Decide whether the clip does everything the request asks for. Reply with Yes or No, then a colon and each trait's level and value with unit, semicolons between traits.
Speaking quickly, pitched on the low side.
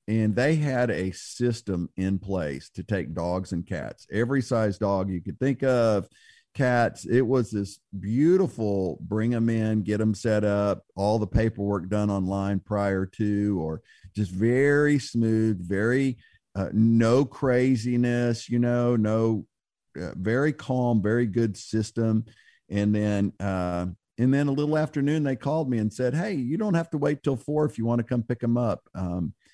No: average, 175 wpm; low, 110 Hz